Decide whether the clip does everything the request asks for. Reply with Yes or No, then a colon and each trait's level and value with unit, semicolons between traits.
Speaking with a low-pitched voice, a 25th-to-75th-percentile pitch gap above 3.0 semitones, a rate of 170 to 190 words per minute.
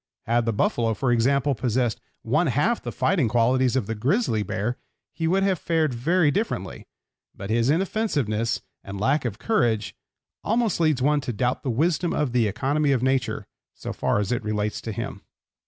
Yes: low, 130 Hz; wide, 5.4 semitones; average, 180 wpm